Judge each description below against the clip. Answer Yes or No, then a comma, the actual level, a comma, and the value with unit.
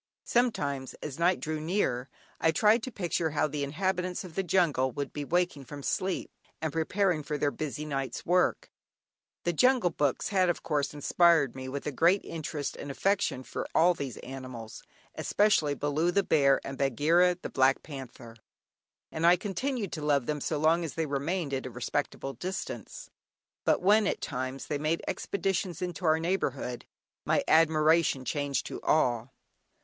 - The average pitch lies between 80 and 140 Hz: No, medium, 155 Hz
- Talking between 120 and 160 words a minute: No, average, 170 wpm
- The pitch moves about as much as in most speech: Yes, average, 4.3 semitones